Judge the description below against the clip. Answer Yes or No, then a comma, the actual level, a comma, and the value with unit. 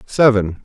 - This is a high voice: No, low, 110 Hz